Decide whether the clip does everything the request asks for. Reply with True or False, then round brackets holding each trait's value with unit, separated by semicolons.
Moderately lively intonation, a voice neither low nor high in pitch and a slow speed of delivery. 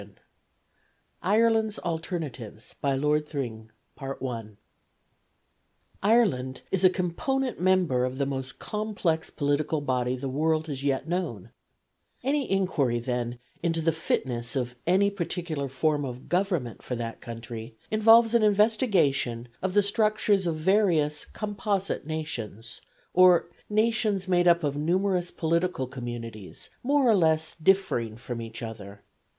False (7.3 semitones; 160 Hz; 125 wpm)